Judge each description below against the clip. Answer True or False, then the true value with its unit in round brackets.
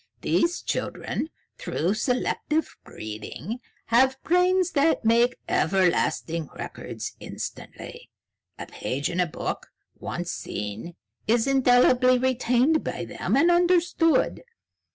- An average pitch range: False (8.7 semitones)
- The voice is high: True (250 Hz)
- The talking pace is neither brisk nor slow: False (105 wpm)